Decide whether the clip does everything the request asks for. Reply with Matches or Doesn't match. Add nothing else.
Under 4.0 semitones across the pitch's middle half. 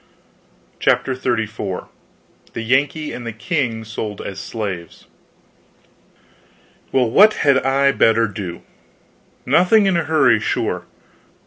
Doesn't match